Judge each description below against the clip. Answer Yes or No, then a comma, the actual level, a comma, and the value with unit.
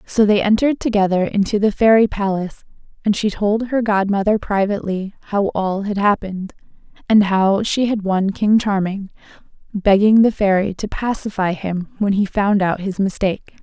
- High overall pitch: Yes, high, 200 Hz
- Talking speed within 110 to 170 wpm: Yes, average, 165 wpm